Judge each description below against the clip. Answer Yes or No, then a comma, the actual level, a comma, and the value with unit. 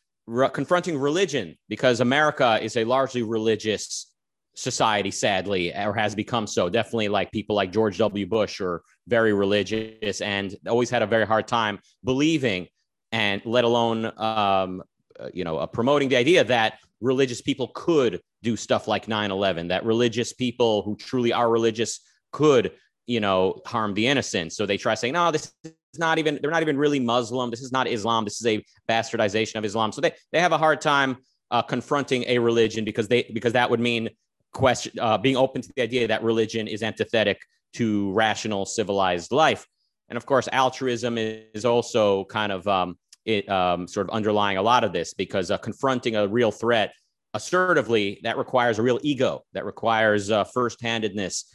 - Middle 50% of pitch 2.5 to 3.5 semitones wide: Yes, average, 2.9 semitones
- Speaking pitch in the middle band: No, low, 115 Hz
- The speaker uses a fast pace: No, average, 180 wpm